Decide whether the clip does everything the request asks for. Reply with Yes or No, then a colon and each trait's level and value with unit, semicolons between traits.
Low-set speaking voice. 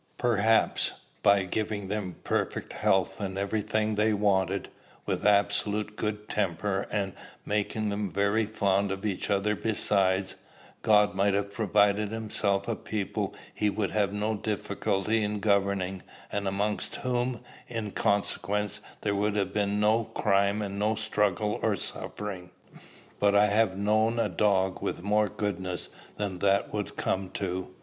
Yes: low, 100 Hz